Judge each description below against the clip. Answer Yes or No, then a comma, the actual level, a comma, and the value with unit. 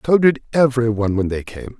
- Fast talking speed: Yes, fast, 235 wpm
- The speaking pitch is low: Yes, low, 120 Hz